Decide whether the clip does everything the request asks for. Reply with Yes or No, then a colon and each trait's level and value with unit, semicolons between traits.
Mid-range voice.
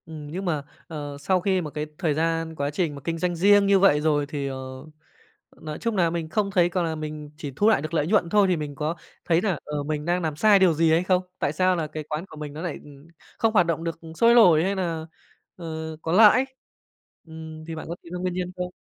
Yes: medium, 165 Hz